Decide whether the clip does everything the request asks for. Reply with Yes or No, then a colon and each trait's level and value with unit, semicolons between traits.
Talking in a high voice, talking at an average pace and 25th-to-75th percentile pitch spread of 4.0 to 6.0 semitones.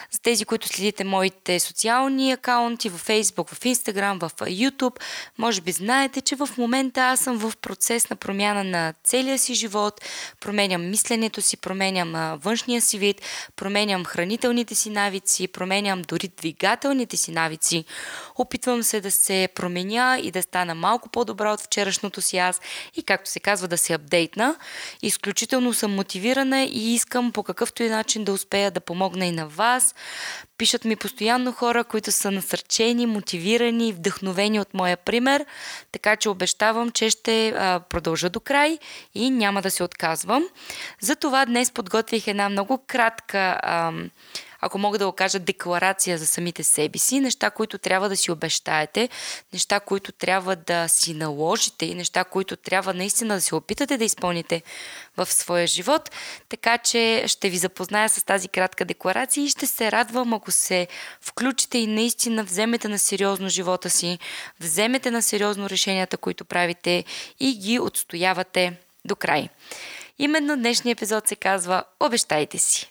Yes: high, 205 Hz; average, 155 wpm; average, 4.3 semitones